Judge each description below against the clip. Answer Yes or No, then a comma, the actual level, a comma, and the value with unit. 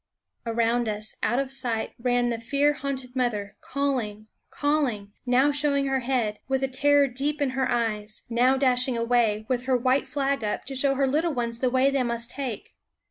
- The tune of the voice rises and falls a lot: No, average, 2.8 semitones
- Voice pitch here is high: Yes, very high, 255 Hz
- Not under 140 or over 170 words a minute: No, average, 190 wpm